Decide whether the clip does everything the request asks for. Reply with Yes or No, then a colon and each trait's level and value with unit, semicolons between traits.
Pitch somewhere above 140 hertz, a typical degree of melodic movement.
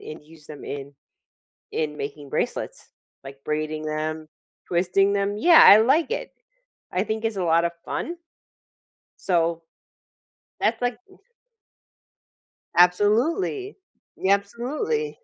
No: high, 190 Hz; wide, 7.2 semitones